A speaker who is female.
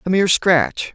No: male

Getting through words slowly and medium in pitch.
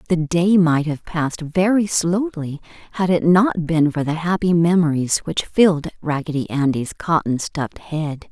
No: average, 160 wpm; medium, 165 Hz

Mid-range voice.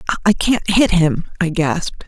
Yes: medium, 180 Hz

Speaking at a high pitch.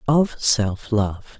No: low, 115 Hz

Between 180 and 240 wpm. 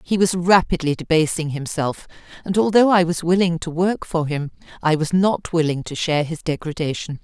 Yes: average, 185 wpm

